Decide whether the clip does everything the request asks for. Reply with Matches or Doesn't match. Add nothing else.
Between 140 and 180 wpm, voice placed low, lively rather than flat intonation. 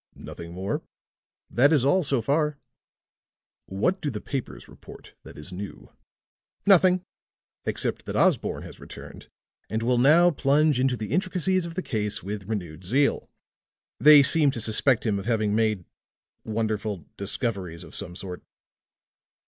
Matches